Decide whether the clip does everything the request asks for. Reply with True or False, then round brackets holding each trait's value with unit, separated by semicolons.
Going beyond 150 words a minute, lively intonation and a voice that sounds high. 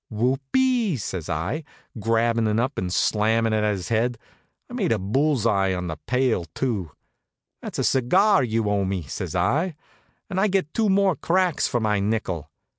False (185 wpm; 7.3 semitones; 115 Hz)